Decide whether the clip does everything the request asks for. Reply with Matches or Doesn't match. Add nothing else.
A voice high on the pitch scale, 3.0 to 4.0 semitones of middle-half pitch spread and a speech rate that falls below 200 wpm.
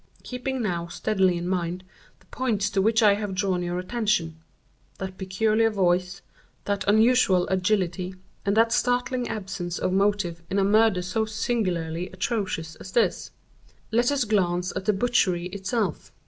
Matches